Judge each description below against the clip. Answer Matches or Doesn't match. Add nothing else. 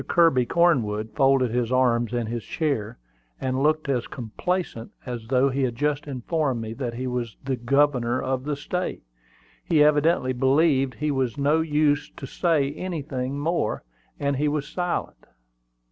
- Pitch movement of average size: Matches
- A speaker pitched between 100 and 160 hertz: Matches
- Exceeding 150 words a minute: Matches